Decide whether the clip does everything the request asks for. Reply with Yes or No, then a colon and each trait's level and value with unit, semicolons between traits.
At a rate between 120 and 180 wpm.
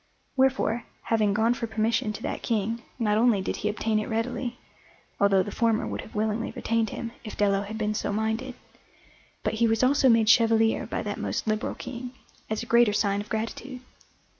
No: average, 190 wpm